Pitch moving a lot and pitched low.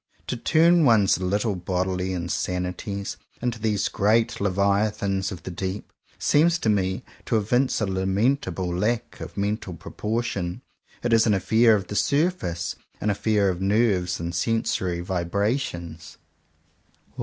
No: average, 3.7 semitones; low, 100 Hz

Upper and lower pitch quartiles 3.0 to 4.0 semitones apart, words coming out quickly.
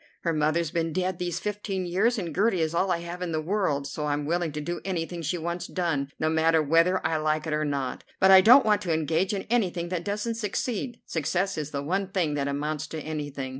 Yes: average, 3.5 semitones; fast, 235 wpm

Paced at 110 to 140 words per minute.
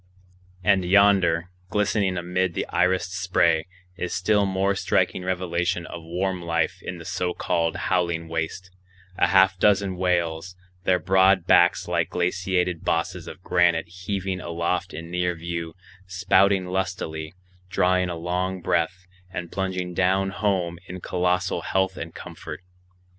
Yes: slow, 135 wpm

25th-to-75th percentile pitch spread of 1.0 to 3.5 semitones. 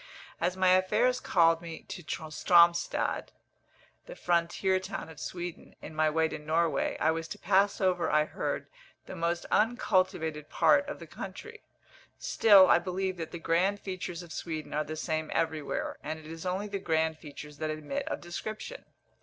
Yes: average, 2.9 semitones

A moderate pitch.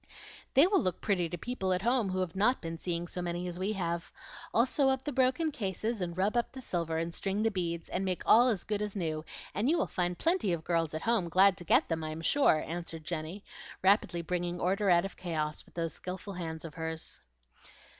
Yes: medium, 180 Hz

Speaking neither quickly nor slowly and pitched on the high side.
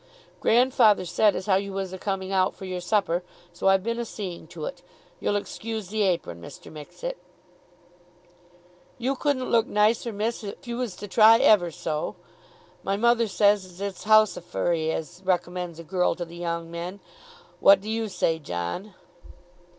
Yes: average, 175 wpm; high, 195 Hz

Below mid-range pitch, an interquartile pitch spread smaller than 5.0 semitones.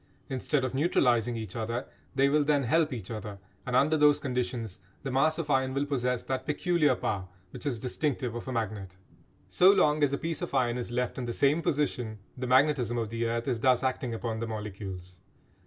Yes: low, 125 Hz; average, 3.8 semitones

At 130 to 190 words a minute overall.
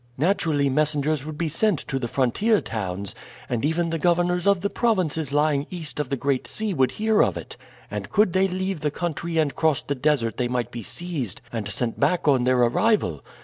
No: fast, 205 wpm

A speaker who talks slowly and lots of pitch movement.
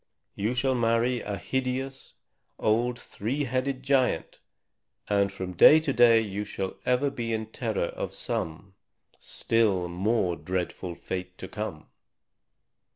No: slow, 130 wpm; average, 4.9 semitones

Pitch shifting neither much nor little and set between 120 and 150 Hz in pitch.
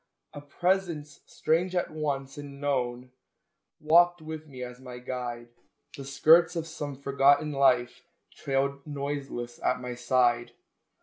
Yes: average, 3.4 semitones; medium, 140 Hz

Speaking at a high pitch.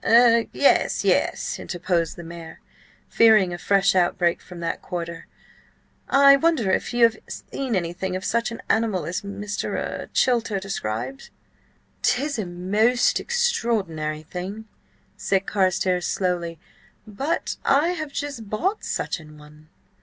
Yes: high, 195 Hz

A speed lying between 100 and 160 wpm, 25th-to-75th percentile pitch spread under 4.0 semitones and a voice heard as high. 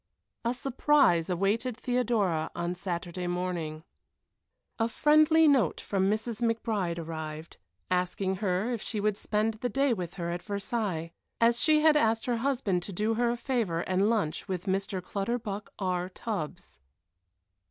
No: average, 150 wpm; average, 4.8 semitones; high, 205 Hz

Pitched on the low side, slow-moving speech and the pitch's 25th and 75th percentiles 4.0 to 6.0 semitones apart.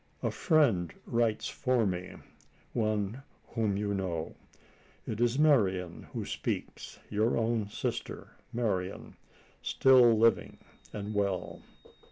No: low, 110 Hz; slow, 110 wpm; average, 3.5 semitones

